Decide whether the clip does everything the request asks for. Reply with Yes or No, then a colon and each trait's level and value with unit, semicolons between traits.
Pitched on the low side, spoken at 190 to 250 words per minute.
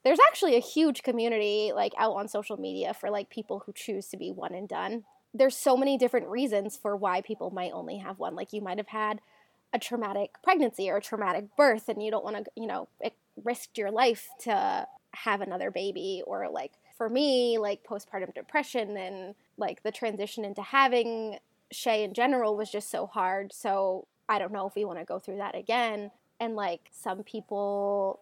No: high, 215 Hz; average, 200 wpm